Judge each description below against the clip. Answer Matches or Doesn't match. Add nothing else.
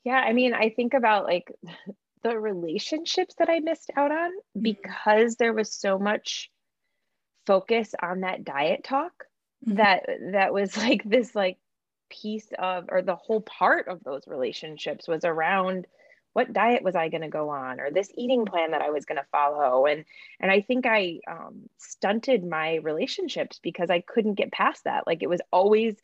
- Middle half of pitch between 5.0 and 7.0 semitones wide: Matches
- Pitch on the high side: Matches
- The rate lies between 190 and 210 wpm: Doesn't match